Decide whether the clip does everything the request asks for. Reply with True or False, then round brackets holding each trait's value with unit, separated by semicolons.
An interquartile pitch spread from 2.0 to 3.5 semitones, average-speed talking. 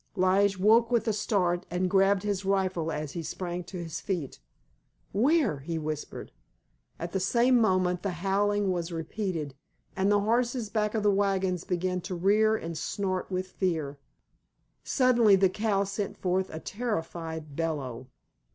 True (3.2 semitones; 155 wpm)